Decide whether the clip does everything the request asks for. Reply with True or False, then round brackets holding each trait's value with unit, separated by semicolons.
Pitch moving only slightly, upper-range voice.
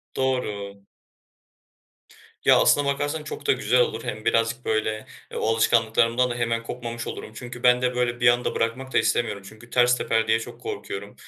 False (2.0 semitones; 120 Hz)